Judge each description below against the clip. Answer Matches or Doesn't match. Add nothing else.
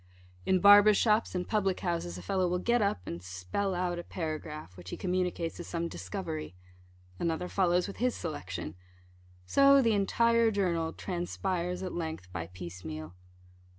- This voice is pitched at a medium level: Matches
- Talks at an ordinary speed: Matches